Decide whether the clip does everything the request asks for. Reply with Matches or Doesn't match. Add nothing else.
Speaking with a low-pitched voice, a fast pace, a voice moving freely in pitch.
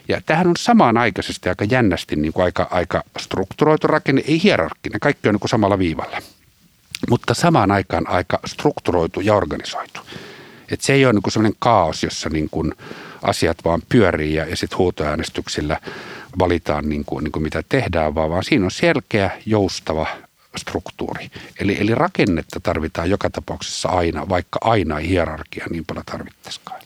Matches